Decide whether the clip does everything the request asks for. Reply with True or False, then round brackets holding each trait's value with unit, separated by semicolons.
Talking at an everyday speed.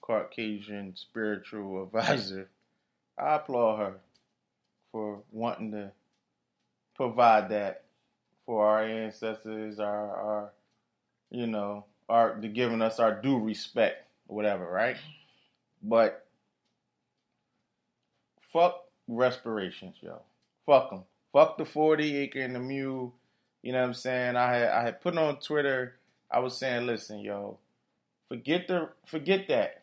False (125 wpm)